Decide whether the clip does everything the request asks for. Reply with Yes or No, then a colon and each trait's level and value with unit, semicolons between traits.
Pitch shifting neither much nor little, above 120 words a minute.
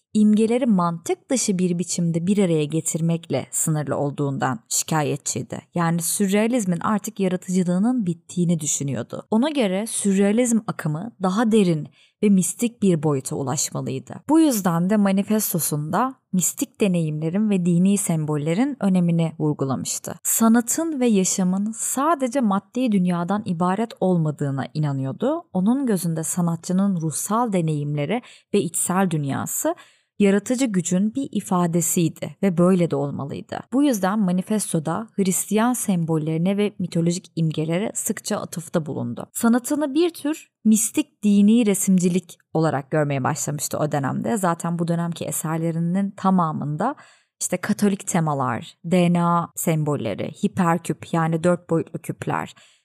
No: average, 4.4 semitones; average, 115 wpm